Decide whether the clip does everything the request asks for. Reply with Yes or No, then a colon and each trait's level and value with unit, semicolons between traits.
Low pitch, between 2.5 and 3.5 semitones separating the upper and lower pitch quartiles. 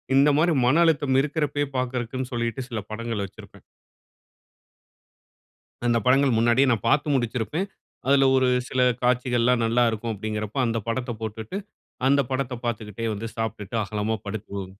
Yes: low, 120 Hz; average, 3.2 semitones